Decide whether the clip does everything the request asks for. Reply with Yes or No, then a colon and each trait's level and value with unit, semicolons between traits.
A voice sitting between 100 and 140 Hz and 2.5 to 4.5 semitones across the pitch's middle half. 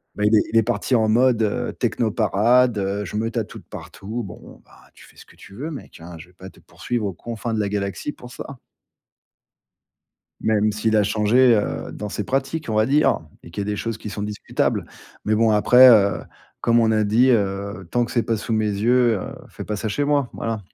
Yes: low, 110 Hz; average, 2.8 semitones